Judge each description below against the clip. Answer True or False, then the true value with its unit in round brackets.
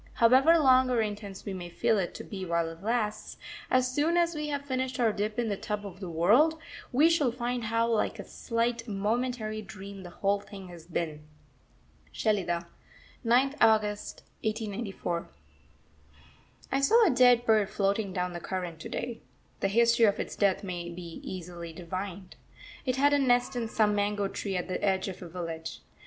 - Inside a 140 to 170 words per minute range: False (180 wpm)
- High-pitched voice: True (210 Hz)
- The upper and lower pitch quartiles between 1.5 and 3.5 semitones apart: False (4.7 semitones)